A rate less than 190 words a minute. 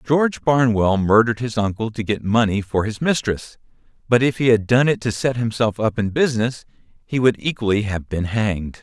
No: average, 195 wpm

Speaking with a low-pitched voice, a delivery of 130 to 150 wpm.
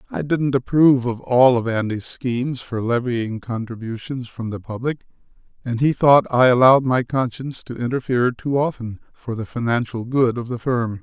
No: low, 125 Hz; average, 175 wpm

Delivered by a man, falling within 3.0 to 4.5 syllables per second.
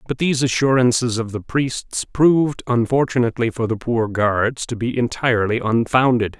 No: male; 5.0 syllables/s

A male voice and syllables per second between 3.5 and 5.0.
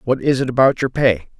No: male; 5.8 syllables/s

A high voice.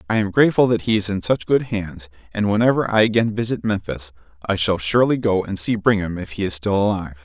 No: low, 100 Hz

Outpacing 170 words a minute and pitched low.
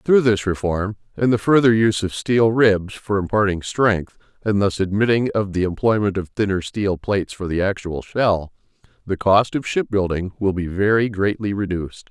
Yes: average, 180 wpm; low, 100 Hz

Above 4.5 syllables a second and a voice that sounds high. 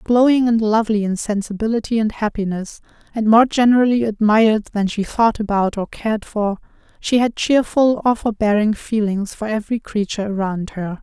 Yes: 5.3 syllables/s; high, 215 Hz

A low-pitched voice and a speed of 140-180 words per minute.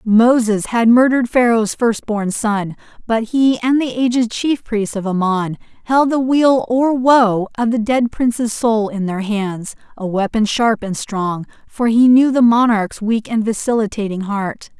No: high, 225 Hz; average, 170 wpm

